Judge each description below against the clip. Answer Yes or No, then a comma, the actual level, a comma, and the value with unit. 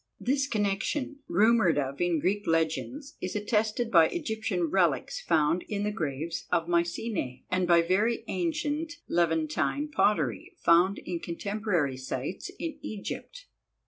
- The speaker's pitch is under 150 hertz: No, medium, 185 Hz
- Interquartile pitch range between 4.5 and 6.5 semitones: Yes, average, 5.3 semitones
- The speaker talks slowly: Yes, slow, 130 wpm